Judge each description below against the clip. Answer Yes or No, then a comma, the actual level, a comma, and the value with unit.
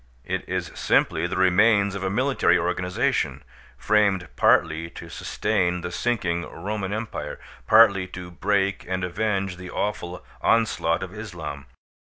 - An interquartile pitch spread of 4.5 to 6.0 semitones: No, average, 3.0 semitones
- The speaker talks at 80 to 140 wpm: Yes, slow, 135 wpm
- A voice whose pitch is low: Yes, very low, 95 Hz